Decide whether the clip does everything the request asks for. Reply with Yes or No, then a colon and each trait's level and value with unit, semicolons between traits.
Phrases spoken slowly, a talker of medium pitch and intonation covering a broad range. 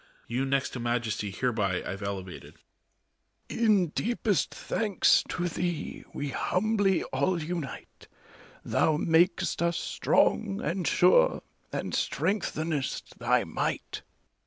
Yes: slow, 110 wpm; medium, 160 Hz; wide, 7.4 semitones